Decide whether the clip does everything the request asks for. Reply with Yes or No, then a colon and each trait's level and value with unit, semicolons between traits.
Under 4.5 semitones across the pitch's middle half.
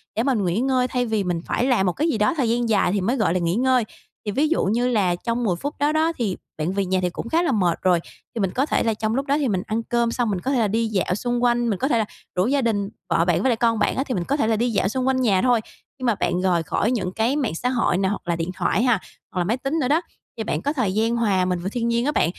No: average, 4.8 semitones